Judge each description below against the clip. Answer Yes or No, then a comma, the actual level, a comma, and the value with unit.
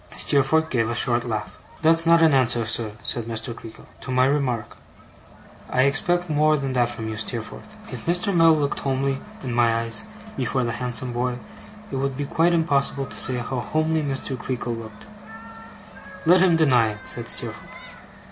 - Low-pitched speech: Yes, low, 130 Hz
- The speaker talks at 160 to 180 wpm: Yes, average, 175 wpm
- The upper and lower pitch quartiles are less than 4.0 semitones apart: No, average, 4.6 semitones